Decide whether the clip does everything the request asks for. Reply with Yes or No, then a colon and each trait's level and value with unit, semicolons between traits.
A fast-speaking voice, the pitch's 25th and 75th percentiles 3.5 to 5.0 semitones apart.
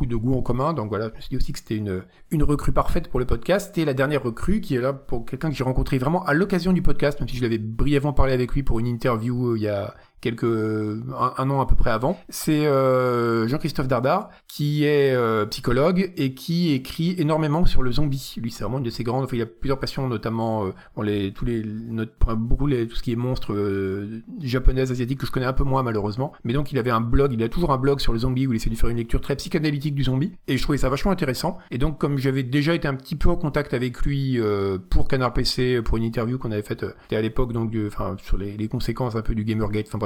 Yes: fast, 265 wpm; average, 3.9 semitones